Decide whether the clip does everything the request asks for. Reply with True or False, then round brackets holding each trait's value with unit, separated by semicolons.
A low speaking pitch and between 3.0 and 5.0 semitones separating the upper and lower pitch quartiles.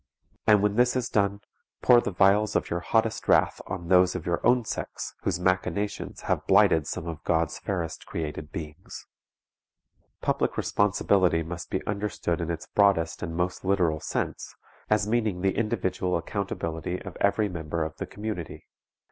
True (90 Hz; 3.6 semitones)